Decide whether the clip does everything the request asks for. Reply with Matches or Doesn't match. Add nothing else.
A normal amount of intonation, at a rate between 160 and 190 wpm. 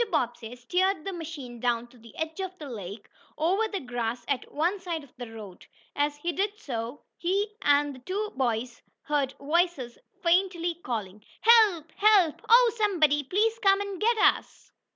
Doesn't match